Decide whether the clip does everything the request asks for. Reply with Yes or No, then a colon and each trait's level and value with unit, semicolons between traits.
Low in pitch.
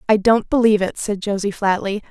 No: high, 205 Hz